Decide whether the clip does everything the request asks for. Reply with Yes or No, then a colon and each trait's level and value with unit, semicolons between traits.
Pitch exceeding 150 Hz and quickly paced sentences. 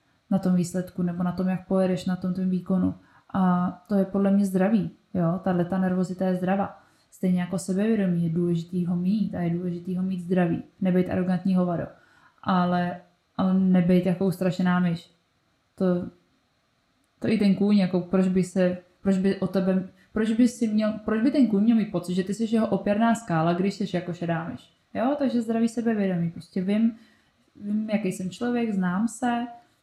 Yes: medium, 185 Hz; fast, 185 wpm